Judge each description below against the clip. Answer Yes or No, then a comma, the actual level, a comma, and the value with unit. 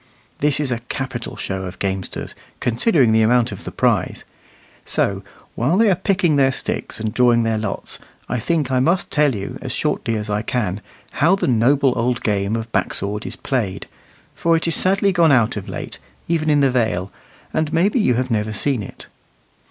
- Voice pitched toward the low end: Yes, low, 125 Hz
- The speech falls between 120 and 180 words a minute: No, average, 195 wpm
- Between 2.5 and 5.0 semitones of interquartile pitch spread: No, wide, 5.6 semitones